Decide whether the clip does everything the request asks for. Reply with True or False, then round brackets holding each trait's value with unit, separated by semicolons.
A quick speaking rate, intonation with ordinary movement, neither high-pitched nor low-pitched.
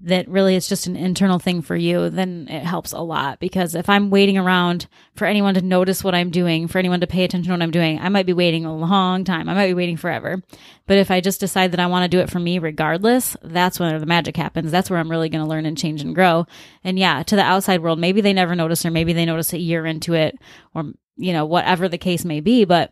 False (270 wpm; 2.0 semitones; 180 Hz)